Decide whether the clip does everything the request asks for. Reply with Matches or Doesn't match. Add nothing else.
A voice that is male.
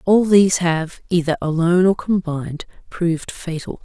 Doesn't match